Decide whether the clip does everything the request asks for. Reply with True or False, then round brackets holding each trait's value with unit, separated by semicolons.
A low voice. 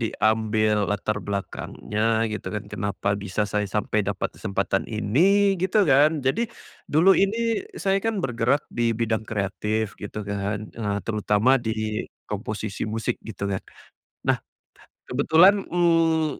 True (110 Hz)